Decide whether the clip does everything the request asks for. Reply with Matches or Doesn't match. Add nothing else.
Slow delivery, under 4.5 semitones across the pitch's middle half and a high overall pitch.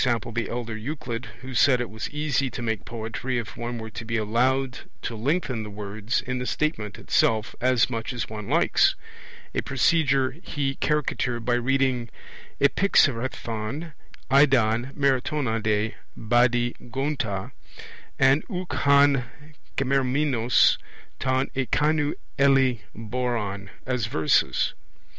Doesn't match